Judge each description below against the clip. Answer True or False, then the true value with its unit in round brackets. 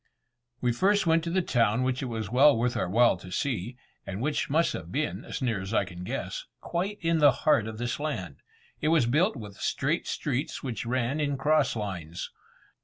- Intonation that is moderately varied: False (5.8 semitones)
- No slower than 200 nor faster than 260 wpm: True (205 wpm)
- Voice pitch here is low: True (125 Hz)